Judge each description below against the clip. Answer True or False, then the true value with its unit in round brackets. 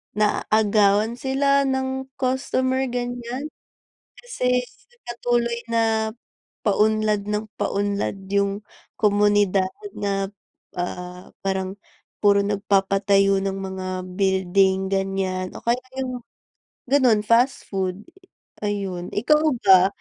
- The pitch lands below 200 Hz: False (205 Hz)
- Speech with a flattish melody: False (3.7 semitones)